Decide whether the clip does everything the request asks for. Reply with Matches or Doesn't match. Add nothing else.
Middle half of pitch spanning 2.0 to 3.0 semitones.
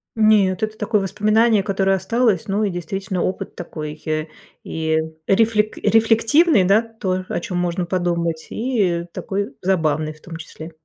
Doesn't match